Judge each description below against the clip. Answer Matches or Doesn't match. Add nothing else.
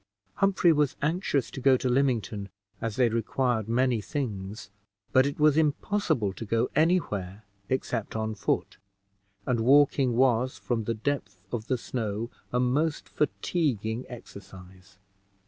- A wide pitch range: Doesn't match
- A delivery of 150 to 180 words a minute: Doesn't match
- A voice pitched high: Doesn't match